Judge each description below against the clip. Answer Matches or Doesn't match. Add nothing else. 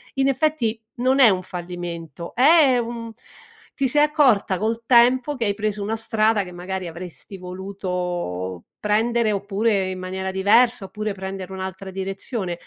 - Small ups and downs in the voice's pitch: Doesn't match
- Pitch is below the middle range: Doesn't match